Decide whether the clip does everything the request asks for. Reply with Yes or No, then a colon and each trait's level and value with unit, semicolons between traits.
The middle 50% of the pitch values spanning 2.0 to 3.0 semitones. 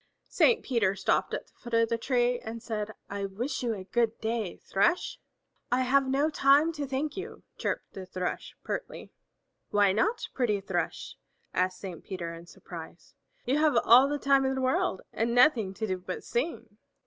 No: wide, 5.5 semitones